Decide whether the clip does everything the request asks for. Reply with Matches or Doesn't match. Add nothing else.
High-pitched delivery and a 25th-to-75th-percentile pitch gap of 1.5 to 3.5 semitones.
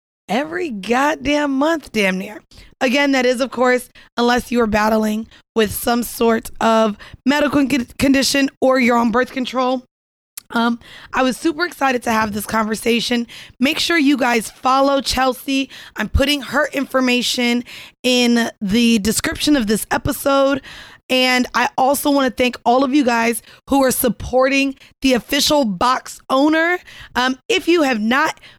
Matches